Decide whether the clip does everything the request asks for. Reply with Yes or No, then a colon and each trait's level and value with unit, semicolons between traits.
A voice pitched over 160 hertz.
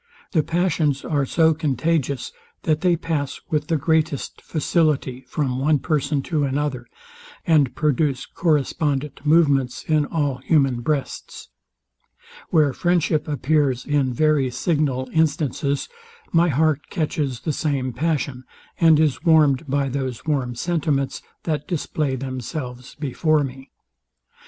No: medium, 145 Hz